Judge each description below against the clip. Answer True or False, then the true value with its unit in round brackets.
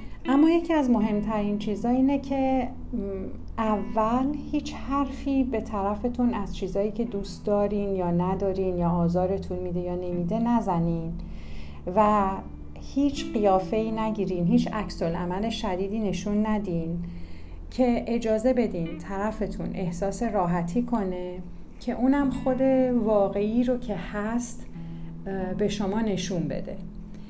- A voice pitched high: True (205 Hz)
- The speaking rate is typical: True (115 wpm)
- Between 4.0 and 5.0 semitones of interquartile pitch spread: True (4.3 semitones)